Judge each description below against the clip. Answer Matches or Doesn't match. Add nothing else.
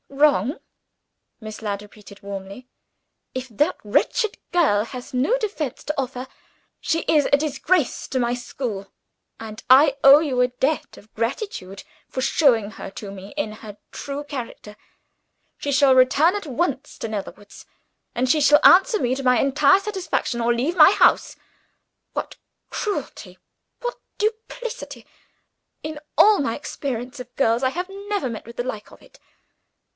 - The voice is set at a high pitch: Matches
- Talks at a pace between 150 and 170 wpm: Matches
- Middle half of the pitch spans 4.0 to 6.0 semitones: Matches